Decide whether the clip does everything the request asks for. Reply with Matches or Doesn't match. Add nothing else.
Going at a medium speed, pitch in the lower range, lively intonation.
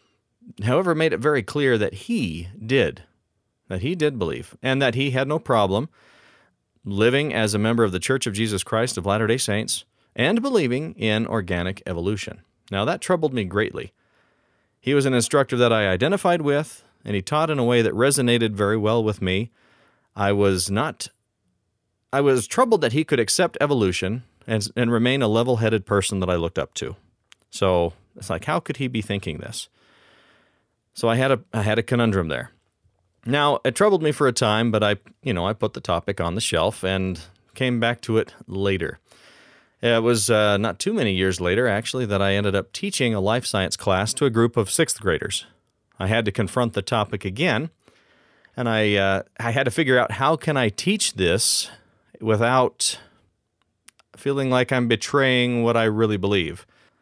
Doesn't match